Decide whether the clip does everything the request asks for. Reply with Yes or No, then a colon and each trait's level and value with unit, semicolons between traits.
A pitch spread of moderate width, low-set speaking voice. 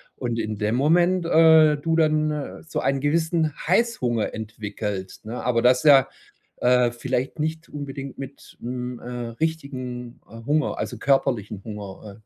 Yes: average, 4.6 semitones; low, 130 Hz